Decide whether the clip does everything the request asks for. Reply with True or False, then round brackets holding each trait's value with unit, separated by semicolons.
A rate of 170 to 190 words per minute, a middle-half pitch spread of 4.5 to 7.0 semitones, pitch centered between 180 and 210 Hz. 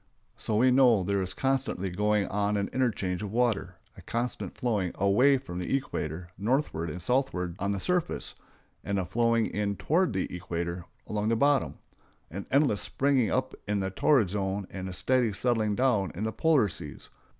False (175 wpm; 5.0 semitones; 105 Hz)